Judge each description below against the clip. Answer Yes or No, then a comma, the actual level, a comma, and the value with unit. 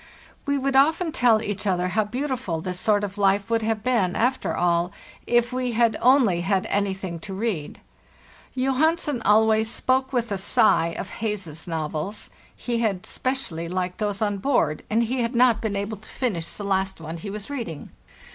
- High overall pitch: Yes, high, 215 Hz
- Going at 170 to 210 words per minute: Yes, average, 180 wpm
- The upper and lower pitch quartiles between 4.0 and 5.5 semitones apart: Yes, average, 4.6 semitones